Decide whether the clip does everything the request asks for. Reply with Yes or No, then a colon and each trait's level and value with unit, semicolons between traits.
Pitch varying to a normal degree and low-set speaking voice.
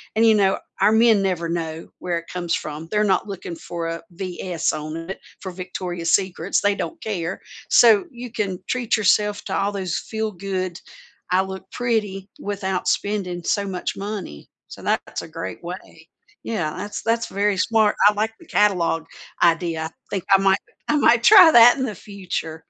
No: average, 3.5 semitones; high, 195 Hz